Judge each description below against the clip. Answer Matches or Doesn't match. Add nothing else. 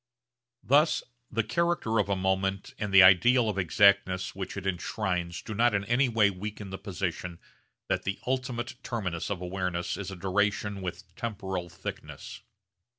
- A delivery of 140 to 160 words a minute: Matches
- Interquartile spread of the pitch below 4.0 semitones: Matches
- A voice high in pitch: Doesn't match